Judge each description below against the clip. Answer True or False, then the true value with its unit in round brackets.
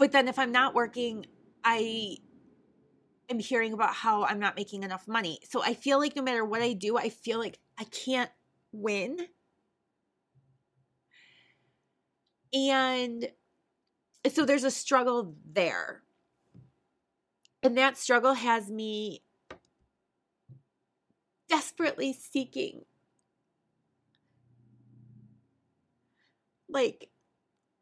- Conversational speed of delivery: False (95 wpm)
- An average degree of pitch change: False (5.9 semitones)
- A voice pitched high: True (230 Hz)